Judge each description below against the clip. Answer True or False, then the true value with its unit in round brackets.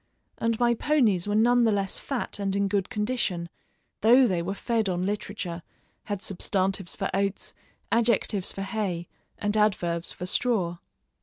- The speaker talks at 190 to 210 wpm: False (155 wpm)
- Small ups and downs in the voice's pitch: False (3.5 semitones)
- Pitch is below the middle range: False (200 Hz)